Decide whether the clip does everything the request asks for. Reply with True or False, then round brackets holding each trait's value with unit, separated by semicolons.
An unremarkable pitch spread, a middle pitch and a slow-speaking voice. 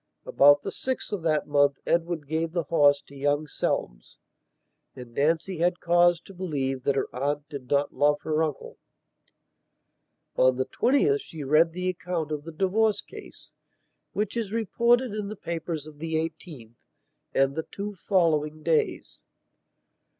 False (3.9 semitones; 160 Hz; 155 wpm)